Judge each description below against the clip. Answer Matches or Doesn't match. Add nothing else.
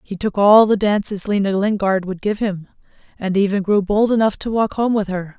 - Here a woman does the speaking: Matches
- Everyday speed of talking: Doesn't match